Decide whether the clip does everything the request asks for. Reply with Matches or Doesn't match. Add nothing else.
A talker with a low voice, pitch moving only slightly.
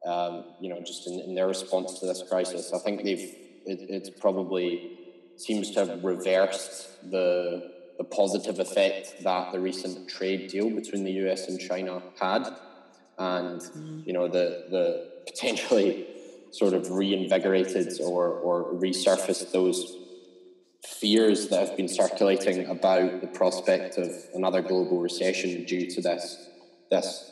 Matches